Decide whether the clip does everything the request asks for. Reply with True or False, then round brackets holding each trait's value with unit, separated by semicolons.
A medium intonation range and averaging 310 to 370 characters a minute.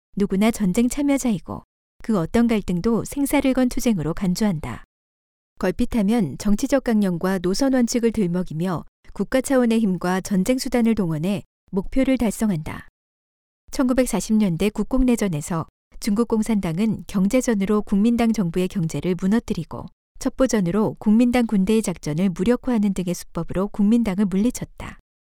True (4.4 semitones; 320 characters per minute)